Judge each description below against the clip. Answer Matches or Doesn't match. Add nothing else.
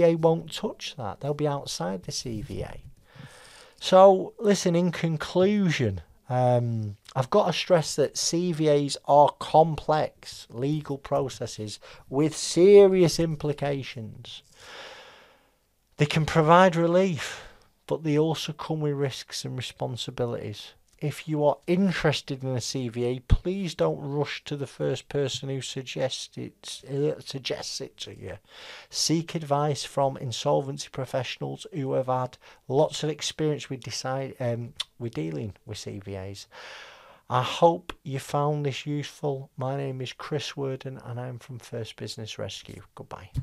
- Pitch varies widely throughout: Doesn't match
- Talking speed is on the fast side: Doesn't match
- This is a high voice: Doesn't match